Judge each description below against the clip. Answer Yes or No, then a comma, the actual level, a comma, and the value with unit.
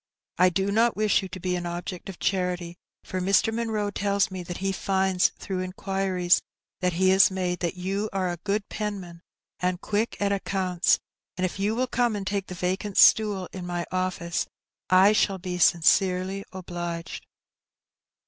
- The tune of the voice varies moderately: No, narrow, 1.8 semitones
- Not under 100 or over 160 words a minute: No, average, 175 wpm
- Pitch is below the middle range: No, medium, 185 Hz